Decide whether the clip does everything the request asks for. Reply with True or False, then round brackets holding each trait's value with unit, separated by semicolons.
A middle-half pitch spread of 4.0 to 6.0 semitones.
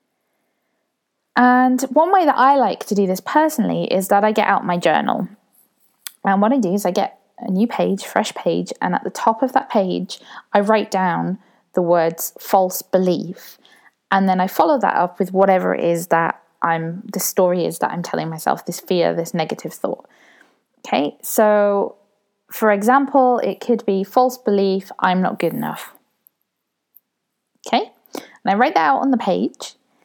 True (4.8 semitones)